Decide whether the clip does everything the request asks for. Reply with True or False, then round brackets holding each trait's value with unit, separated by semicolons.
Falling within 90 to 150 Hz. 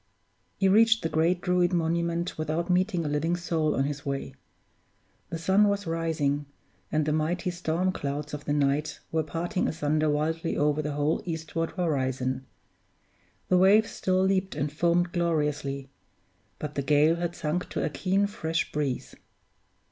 False (160 Hz)